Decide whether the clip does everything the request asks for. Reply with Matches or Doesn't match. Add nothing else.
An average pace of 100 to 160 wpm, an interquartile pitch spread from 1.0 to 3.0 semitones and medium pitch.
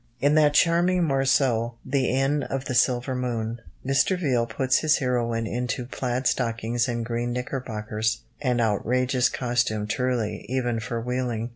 Doesn't match